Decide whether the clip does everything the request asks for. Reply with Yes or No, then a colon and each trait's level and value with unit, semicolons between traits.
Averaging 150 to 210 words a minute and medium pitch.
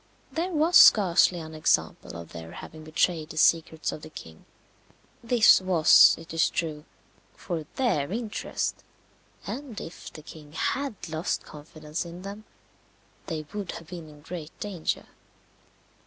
No: average, 140 wpm; medium, 165 Hz